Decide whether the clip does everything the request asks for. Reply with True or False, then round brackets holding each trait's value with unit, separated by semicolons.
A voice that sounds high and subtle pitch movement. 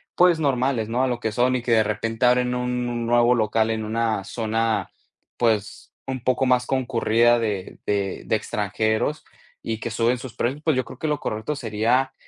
False (120 Hz; 2.3 semitones)